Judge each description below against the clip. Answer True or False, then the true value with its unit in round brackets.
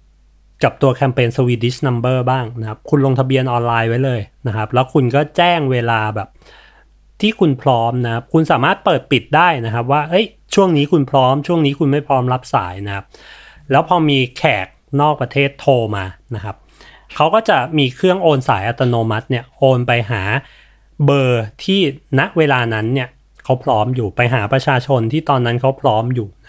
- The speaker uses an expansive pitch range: False (3.8 semitones)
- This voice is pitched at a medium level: False (130 Hz)